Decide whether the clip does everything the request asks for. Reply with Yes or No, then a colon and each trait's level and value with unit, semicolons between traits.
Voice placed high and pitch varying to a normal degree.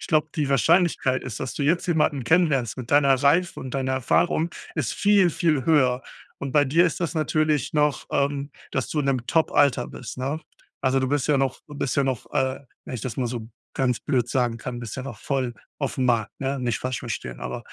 No: low, 135 Hz; average, 3.0 semitones